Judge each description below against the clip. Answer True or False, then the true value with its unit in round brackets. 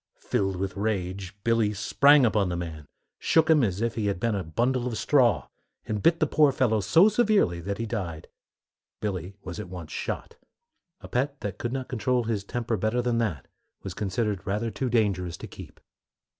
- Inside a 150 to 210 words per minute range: True (190 wpm)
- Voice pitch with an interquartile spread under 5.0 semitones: True (4.4 semitones)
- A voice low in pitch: True (110 Hz)